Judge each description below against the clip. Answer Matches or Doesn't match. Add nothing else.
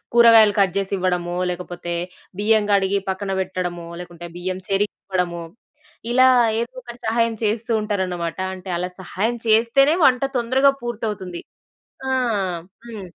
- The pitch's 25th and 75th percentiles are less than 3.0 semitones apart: Doesn't match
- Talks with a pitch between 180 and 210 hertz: Matches